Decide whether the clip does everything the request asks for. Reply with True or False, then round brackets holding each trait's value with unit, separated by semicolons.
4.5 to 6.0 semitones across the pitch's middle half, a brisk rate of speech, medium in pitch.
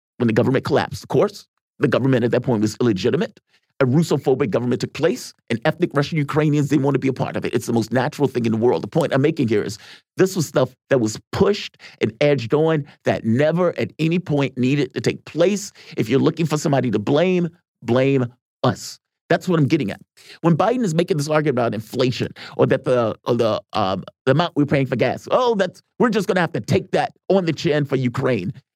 True (4.8 semitones; 225 wpm; 145 Hz)